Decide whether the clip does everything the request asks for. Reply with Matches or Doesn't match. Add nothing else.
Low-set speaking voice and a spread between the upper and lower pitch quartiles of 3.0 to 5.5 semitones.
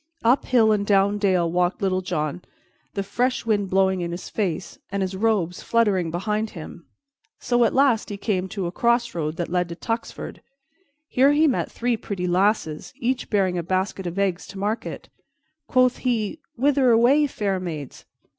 Doesn't match